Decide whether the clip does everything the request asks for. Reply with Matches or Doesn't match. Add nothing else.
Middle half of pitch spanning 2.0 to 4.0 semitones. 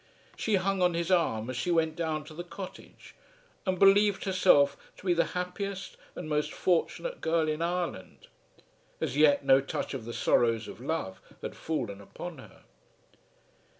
Doesn't match